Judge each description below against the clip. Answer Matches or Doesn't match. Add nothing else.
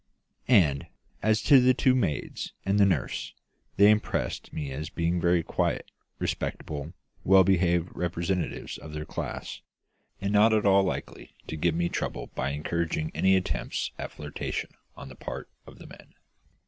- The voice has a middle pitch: Doesn't match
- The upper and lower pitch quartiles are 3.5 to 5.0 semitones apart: Matches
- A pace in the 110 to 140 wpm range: Doesn't match